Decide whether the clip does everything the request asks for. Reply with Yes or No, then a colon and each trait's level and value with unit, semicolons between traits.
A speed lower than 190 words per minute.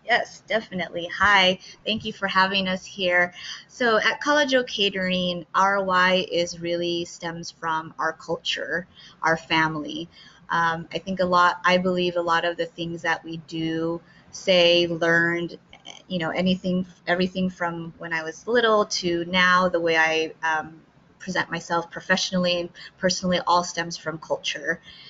Yes: average, 155 wpm